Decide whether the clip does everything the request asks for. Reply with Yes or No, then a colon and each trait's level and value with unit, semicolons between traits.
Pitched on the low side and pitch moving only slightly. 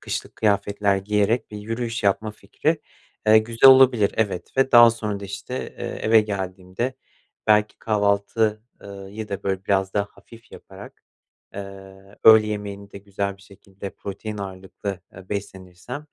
Yes: low, 100 Hz; narrow, 2.0 semitones